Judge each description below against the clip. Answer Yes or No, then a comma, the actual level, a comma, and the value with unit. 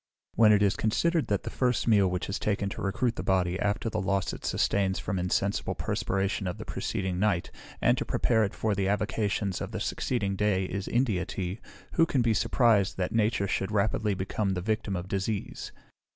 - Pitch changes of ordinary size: No, narrow, 2.2 semitones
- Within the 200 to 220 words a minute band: Yes, fast, 205 wpm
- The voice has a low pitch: Yes, low, 100 Hz